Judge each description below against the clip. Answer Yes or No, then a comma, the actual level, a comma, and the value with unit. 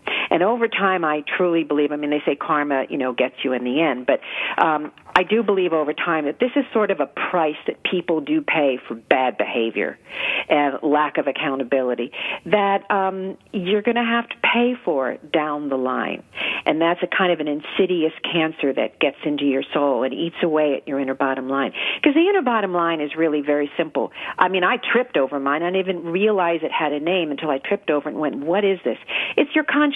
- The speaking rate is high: Yes, fast, 225 wpm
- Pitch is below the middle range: No, medium, 160 Hz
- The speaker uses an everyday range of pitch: Yes, average, 5.0 semitones